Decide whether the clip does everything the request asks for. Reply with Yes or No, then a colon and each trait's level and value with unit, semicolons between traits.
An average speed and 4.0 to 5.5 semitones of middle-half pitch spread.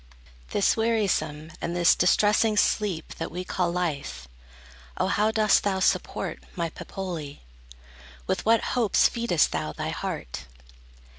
No: slow, 130 wpm; average, 4.8 semitones